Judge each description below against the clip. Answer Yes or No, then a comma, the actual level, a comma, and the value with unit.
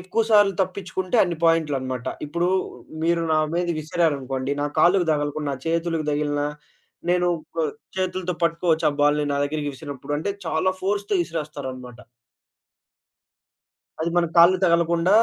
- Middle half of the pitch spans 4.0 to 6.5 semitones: No, average, 3.4 semitones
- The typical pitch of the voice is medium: Yes, medium, 165 Hz